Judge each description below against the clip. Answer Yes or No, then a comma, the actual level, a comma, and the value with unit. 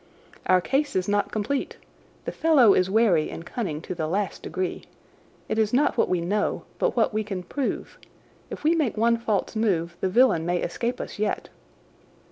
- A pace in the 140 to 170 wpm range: No, average, 185 wpm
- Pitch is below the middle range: No, high, 210 Hz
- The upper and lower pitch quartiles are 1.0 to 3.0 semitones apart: No, average, 4.4 semitones